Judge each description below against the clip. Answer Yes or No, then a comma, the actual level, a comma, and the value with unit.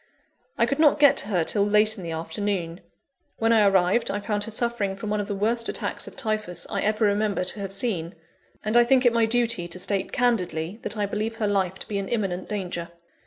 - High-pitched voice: Yes, high, 205 Hz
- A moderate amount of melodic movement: Yes, average, 3.0 semitones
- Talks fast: Yes, fast, 230 wpm